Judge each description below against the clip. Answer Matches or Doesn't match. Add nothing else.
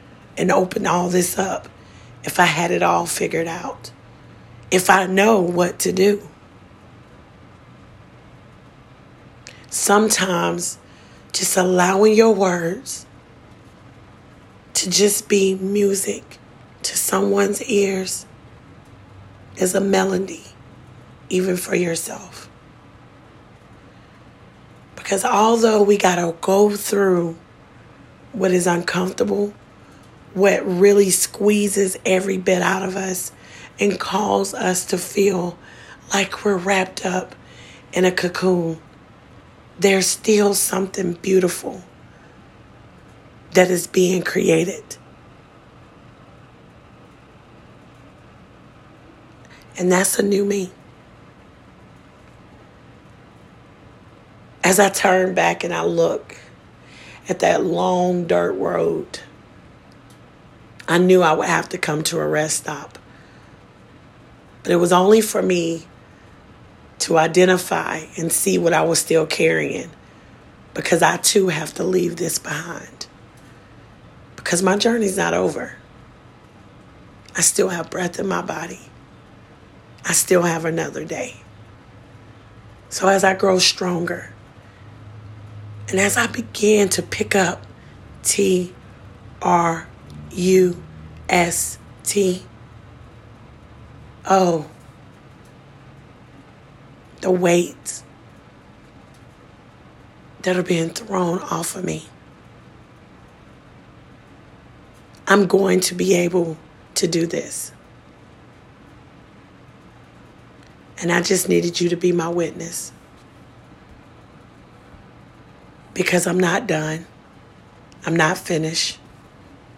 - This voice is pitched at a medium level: Matches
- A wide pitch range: Matches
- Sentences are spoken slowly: Matches